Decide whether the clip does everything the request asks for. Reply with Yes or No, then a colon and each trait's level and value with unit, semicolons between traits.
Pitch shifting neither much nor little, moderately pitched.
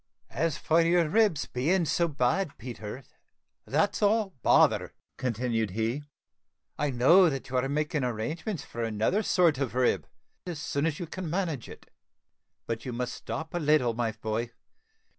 No: wide, 5.7 semitones; medium, 145 Hz